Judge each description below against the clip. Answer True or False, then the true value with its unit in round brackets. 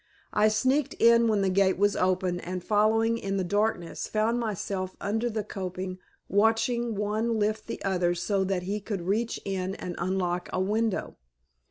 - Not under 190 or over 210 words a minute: False (170 wpm)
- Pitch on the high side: True (205 Hz)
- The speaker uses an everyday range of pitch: True (3.0 semitones)